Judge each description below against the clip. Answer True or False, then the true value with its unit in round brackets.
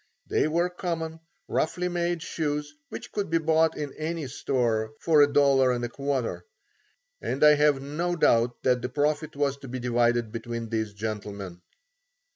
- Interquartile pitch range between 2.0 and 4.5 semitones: False (4.9 semitones)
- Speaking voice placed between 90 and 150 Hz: True (140 Hz)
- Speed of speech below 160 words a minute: True (145 wpm)